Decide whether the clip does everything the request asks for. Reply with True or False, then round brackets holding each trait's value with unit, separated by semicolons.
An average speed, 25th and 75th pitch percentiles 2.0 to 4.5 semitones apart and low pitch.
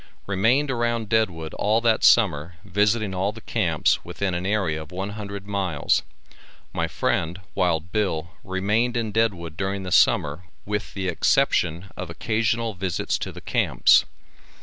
True (150 wpm; 4.0 semitones; 100 Hz)